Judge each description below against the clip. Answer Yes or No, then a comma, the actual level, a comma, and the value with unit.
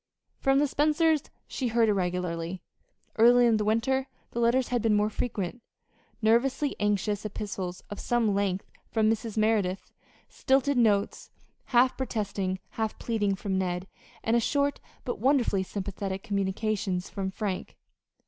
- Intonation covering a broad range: No, average, 3.7 semitones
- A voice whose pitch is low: No, high, 215 Hz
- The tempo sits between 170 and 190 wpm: No, slow, 135 wpm